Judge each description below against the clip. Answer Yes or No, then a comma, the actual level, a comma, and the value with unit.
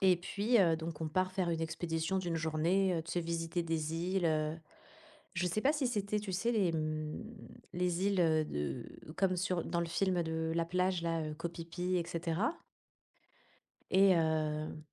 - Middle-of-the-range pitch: Yes, medium, 170 Hz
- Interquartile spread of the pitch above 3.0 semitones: No, narrow, 2.5 semitones